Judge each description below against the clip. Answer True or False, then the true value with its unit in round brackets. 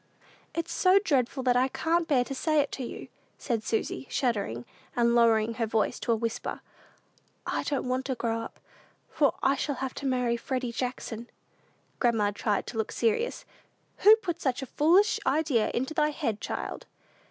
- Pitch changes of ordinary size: True (4.2 semitones)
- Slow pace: False (175 wpm)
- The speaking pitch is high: True (255 Hz)